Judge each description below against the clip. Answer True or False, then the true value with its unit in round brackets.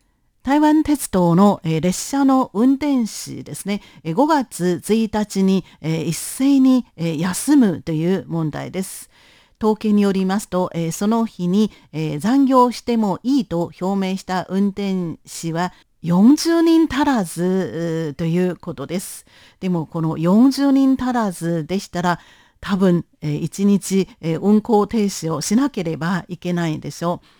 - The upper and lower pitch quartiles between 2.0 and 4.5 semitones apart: False (5.3 semitones)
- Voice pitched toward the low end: False (190 Hz)